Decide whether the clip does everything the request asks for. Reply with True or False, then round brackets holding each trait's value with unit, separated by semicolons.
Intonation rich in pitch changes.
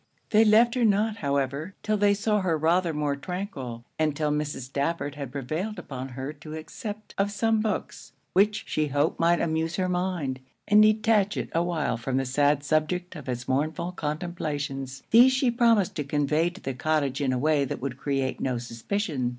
True (6.2 semitones)